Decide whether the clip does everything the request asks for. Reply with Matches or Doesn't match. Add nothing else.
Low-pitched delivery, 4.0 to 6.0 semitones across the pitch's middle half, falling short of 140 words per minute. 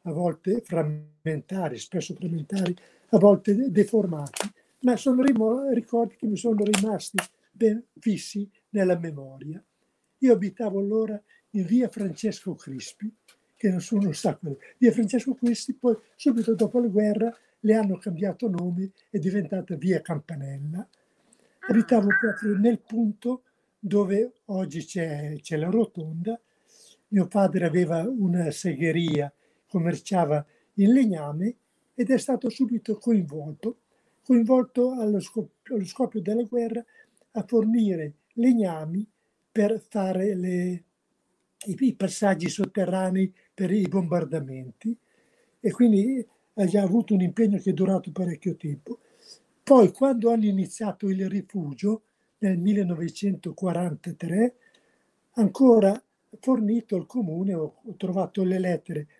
Doesn't match